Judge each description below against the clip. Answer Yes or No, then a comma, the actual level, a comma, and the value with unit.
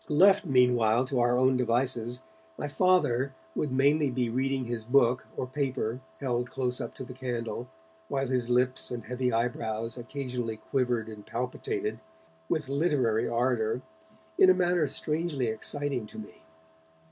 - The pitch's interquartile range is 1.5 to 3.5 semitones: Yes, narrow, 2.5 semitones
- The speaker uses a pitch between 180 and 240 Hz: No, low, 125 Hz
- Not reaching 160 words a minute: Yes, average, 145 wpm